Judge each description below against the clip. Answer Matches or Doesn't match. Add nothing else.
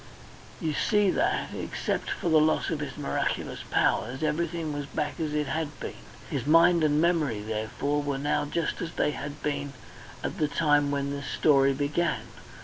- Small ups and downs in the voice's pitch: Matches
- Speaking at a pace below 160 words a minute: Doesn't match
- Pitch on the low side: Doesn't match